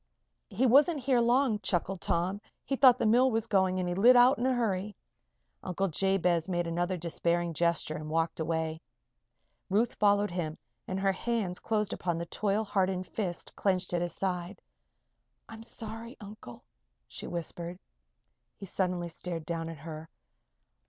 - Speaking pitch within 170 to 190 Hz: Yes, medium, 185 Hz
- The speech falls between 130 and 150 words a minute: No, average, 160 wpm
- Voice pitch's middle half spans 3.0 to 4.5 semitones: Yes, average, 4.2 semitones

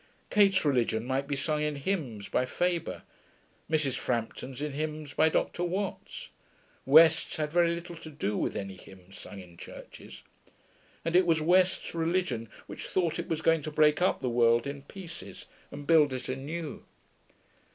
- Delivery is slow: No, average, 165 wpm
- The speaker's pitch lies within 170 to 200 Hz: No, medium, 150 Hz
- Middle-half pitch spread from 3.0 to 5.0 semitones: Yes, average, 4.7 semitones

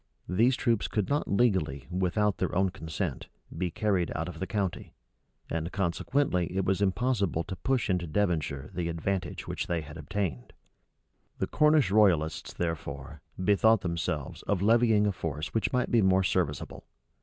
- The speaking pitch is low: Yes, very low, 95 Hz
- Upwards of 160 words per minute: No, average, 155 wpm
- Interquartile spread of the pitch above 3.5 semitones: Yes, average, 4.1 semitones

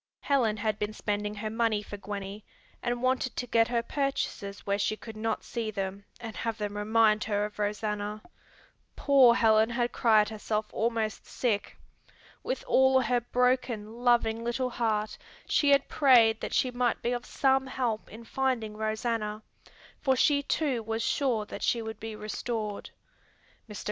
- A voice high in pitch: Yes, high, 225 Hz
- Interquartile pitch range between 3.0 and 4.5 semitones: No, narrow, 2.6 semitones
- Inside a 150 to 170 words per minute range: Yes, average, 165 wpm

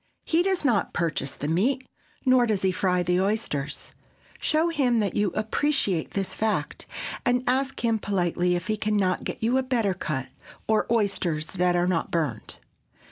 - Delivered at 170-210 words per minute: Yes, average, 175 wpm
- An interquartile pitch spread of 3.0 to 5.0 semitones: No, wide, 5.5 semitones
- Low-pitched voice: No, high, 205 Hz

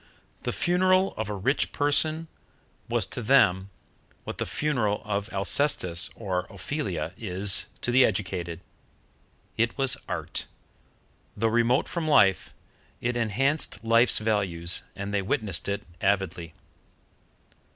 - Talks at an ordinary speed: No, slow, 120 wpm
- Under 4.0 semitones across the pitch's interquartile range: No, wide, 5.5 semitones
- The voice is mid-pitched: No, low, 105 Hz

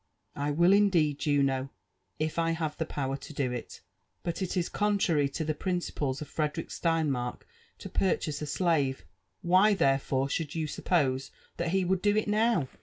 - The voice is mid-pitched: Yes, medium, 155 Hz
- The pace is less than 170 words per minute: No, average, 185 wpm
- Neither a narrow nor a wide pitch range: Yes, average, 4.3 semitones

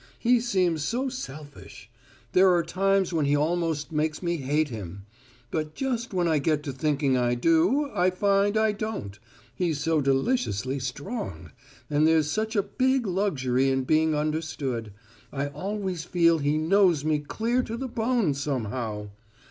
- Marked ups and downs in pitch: Yes, wide, 6.1 semitones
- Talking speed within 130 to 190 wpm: Yes, average, 155 wpm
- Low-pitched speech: No, medium, 160 Hz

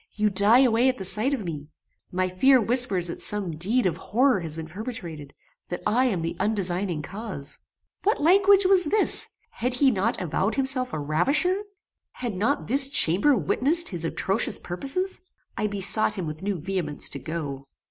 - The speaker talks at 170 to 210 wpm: Yes, average, 175 wpm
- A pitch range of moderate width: No, wide, 7.0 semitones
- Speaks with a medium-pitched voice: No, high, 205 Hz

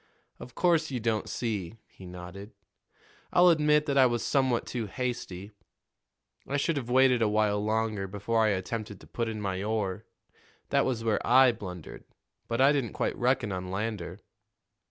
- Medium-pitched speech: No, low, 115 Hz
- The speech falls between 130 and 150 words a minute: No, average, 170 wpm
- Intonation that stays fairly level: No, average, 3.9 semitones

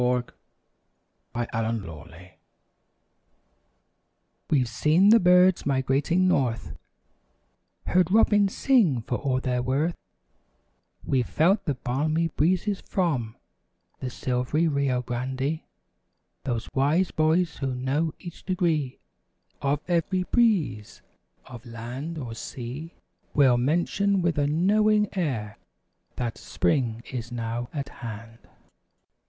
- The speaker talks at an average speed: No, slow, 110 wpm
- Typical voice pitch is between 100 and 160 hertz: Yes, medium, 140 Hz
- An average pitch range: No, wide, 5.9 semitones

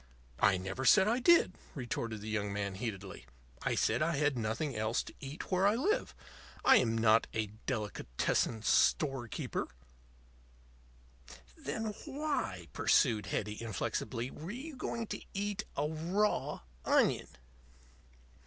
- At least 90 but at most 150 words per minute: Yes, slow, 135 wpm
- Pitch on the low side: Yes, low, 130 Hz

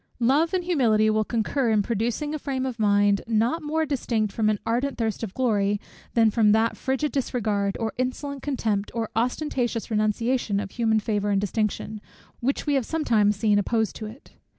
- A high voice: Yes, high, 225 Hz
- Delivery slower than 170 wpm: No, average, 180 wpm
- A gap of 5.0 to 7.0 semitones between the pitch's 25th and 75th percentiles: No, average, 3.7 semitones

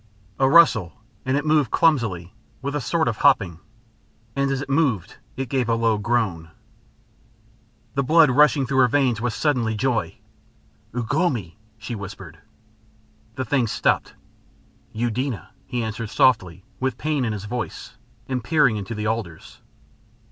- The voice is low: Yes, low, 120 Hz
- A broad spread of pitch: No, average, 4.3 semitones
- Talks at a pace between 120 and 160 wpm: Yes, average, 150 wpm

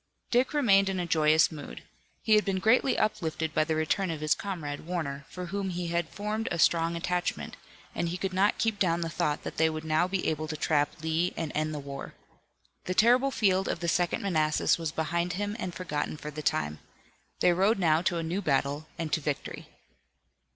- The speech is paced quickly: Yes, fast, 210 wpm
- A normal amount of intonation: Yes, average, 3.5 semitones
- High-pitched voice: No, medium, 170 Hz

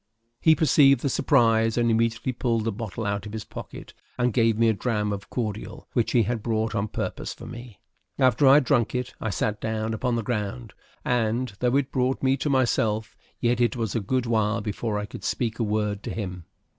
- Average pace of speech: No, fast, 215 wpm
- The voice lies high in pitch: No, low, 115 Hz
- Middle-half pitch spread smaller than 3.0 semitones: Yes, narrow, 2.5 semitones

